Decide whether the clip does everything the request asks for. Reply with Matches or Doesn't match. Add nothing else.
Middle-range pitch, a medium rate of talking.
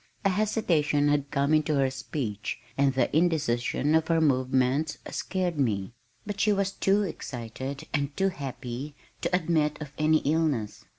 Matches